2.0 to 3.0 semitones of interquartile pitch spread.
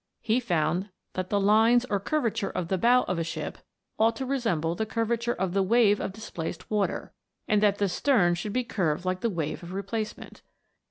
No: average, 4.0 semitones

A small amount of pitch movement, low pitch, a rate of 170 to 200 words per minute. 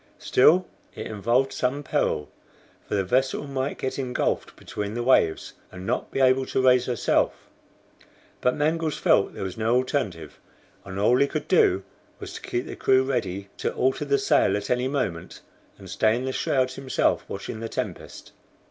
No: average, 4.5 semitones; low, 125 Hz; average, 175 wpm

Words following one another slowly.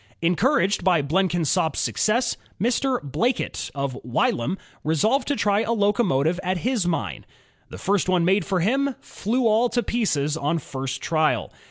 No: average, 150 wpm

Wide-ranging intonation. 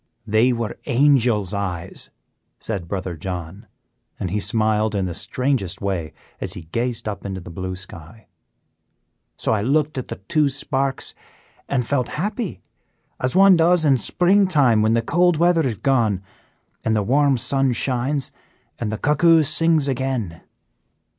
Yes: wide, 6.1 semitones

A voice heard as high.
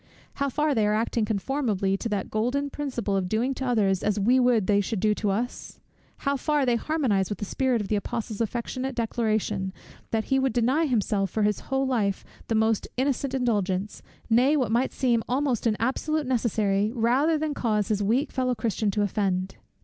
Yes: high, 230 Hz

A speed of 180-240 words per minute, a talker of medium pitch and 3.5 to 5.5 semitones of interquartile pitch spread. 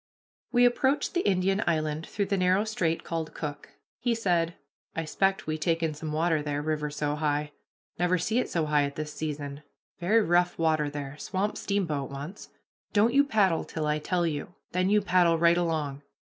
Yes: average, 185 wpm; medium, 165 Hz; average, 4.1 semitones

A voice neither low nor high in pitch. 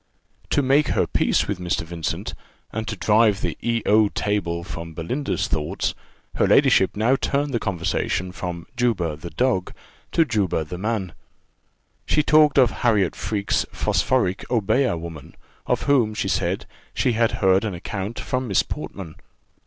No: low, 105 Hz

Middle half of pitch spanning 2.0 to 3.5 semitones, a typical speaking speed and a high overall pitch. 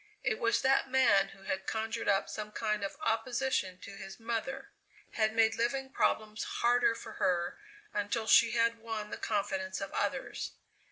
Yes: average, 2.7 semitones; average, 165 wpm; high, 220 Hz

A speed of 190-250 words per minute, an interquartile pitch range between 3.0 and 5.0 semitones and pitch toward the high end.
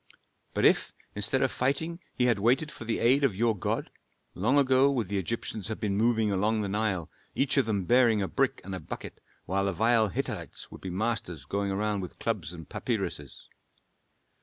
No: average, 195 wpm; average, 3.8 semitones; low, 110 Hz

